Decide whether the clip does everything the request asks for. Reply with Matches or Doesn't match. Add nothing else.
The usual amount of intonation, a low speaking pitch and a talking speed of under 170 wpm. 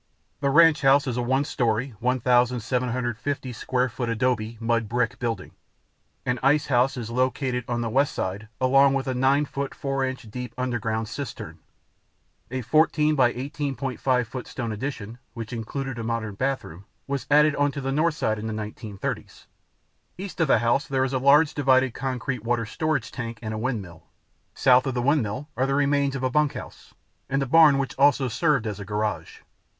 Doesn't match